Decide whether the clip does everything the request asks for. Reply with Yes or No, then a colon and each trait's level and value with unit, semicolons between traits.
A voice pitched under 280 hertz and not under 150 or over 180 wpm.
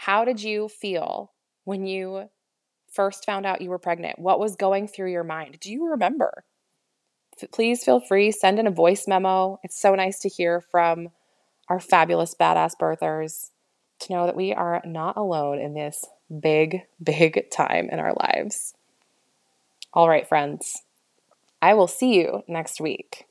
Yes: medium, 185 Hz; average, 165 wpm